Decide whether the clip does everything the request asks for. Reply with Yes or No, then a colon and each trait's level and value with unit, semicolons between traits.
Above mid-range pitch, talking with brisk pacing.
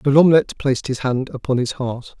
No: low, 135 Hz; fast, 220 wpm